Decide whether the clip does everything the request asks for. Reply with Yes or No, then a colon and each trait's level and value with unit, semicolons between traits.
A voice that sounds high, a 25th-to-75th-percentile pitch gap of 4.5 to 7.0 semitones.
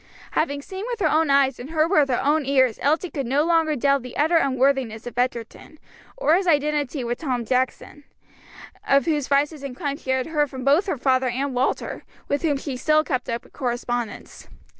No: very high, 280 Hz; average, 3.2 semitones